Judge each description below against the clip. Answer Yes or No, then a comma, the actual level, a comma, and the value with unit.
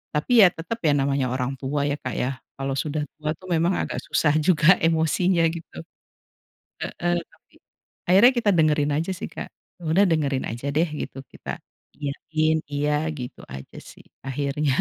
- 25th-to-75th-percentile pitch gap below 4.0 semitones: Yes, average, 3.1 semitones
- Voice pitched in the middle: Yes, medium, 150 Hz